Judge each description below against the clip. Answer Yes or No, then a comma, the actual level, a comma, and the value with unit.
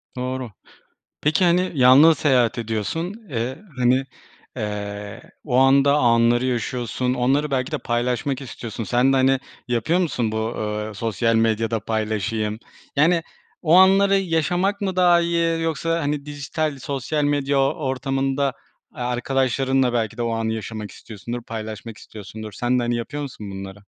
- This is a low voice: Yes, low, 125 Hz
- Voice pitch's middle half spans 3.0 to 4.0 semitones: No, average, 4.5 semitones